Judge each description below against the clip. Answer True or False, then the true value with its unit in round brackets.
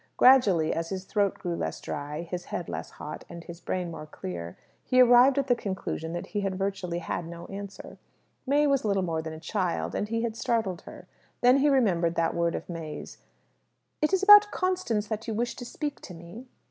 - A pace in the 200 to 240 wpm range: True (205 wpm)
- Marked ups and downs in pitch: True (6.3 semitones)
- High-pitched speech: True (195 Hz)